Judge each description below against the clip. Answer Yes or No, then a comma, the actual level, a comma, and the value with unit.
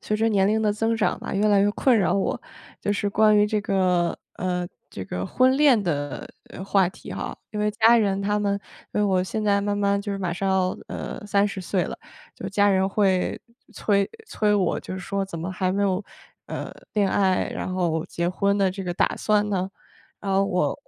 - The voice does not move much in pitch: Yes, narrow, 1.9 semitones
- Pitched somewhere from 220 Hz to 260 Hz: No, high, 200 Hz